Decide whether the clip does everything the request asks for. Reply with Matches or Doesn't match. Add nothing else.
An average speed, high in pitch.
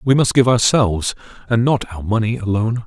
Doesn't match